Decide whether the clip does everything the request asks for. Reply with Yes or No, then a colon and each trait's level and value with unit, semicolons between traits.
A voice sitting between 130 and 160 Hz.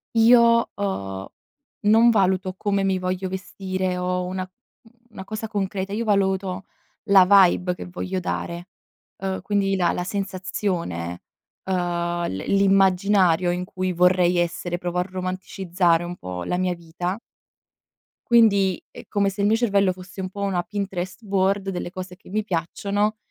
No: medium, 185 Hz